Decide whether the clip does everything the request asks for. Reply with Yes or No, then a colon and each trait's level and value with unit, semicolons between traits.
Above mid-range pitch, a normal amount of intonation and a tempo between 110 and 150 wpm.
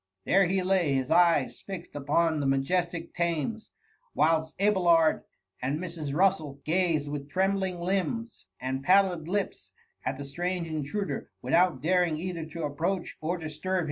No: medium, 170 Hz; average, 3.5 semitones; average, 145 wpm